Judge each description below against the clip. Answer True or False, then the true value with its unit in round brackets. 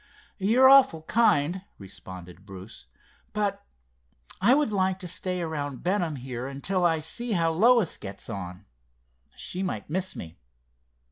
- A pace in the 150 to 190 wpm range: False (135 wpm)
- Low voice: False (165 Hz)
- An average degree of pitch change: False (8.0 semitones)